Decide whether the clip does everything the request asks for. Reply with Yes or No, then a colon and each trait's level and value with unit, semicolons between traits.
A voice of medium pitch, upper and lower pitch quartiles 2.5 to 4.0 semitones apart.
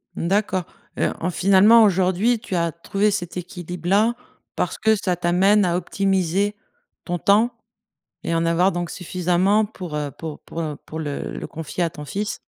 Yes: medium, 180 Hz; average, 3.1 semitones